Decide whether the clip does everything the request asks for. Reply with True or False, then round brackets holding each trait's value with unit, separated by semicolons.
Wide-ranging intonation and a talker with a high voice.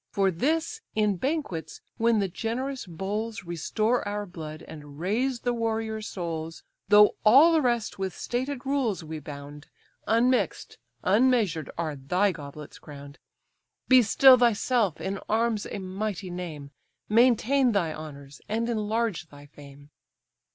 True (6.6 semitones; 205 Hz)